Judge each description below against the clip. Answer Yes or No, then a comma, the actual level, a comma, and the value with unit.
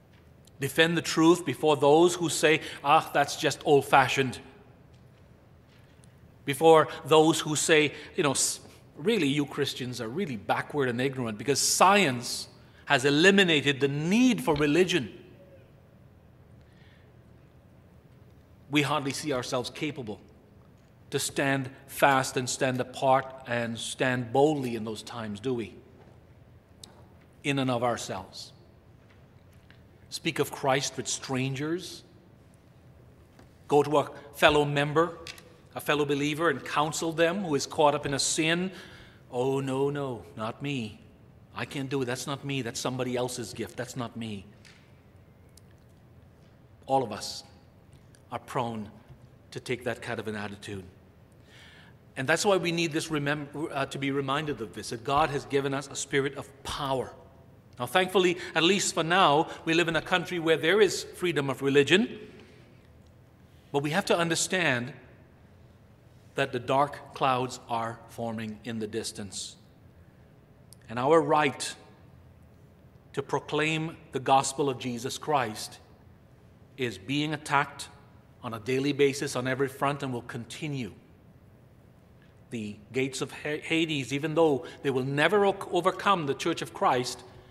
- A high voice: No, low, 135 Hz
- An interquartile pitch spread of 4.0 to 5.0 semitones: Yes, average, 4.3 semitones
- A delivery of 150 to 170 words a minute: No, average, 140 wpm